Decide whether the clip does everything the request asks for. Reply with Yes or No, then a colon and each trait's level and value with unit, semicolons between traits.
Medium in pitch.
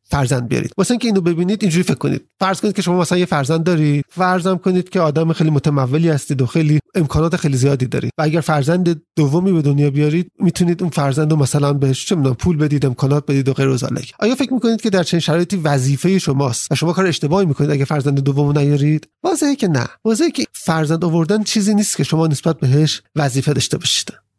Yes: medium, 160 Hz